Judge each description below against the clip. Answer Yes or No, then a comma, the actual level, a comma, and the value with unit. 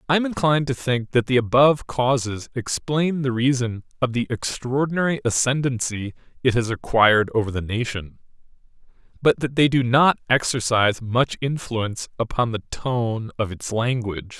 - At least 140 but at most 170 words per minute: Yes, average, 150 wpm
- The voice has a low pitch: Yes, low, 125 Hz